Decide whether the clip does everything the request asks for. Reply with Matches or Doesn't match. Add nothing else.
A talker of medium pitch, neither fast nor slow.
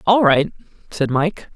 Matches